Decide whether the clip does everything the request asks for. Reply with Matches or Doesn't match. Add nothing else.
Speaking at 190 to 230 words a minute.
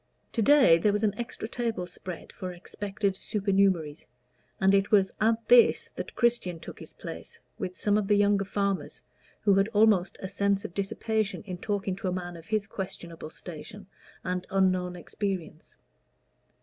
Doesn't match